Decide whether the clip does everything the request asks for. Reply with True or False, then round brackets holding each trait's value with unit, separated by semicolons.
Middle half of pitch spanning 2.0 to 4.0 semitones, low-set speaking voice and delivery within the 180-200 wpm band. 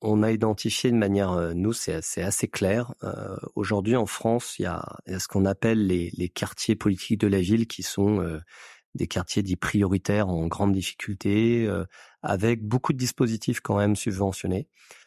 True (2.9 semitones; 105 Hz; 185 wpm)